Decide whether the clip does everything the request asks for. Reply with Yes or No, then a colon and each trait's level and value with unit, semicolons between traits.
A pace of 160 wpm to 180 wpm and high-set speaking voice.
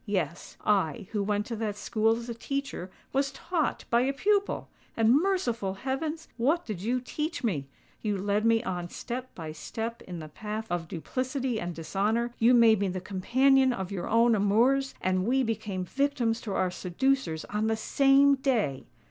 Yes: average, 175 wpm; high, 225 Hz